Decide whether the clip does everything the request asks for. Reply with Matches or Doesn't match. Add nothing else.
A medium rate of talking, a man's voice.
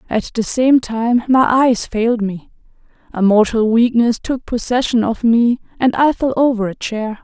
Doesn't match